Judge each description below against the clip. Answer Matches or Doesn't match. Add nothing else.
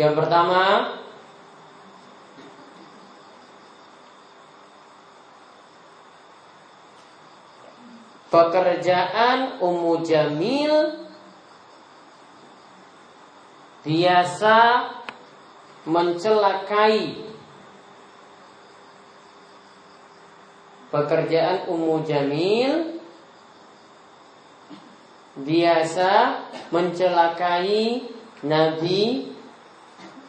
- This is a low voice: Doesn't match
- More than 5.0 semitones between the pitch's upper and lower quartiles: Matches